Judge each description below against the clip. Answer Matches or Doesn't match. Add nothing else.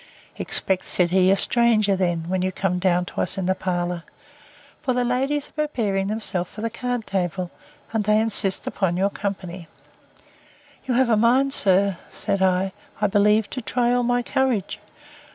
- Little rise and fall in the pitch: Doesn't match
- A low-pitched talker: Doesn't match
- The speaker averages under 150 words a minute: Doesn't match